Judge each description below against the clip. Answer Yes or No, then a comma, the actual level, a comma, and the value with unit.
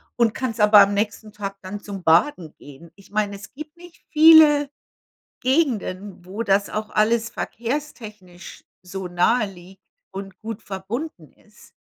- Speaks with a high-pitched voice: Yes, high, 210 Hz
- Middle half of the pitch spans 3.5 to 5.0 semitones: Yes, average, 3.8 semitones